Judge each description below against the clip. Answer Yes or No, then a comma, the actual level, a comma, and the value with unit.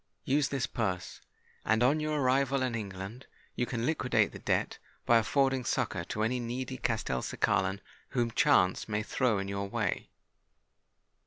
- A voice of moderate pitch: No, low, 120 Hz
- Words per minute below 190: Yes, average, 150 wpm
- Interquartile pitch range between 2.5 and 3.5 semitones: No, average, 4.6 semitones